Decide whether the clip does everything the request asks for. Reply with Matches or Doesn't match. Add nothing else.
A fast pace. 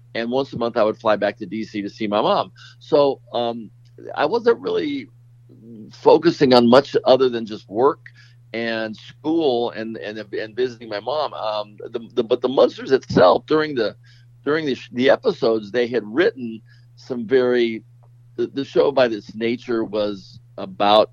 Doesn't match